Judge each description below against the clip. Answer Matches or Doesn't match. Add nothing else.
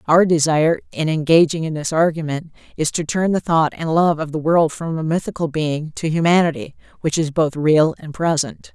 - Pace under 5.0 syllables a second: Doesn't match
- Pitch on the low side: Doesn't match